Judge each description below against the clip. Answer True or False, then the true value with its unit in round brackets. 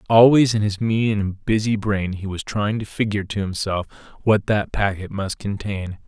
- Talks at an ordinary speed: True (190 wpm)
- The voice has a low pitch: True (105 Hz)